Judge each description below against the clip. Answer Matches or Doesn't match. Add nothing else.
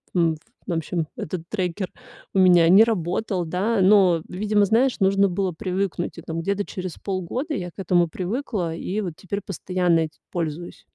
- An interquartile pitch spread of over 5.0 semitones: Doesn't match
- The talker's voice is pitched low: Doesn't match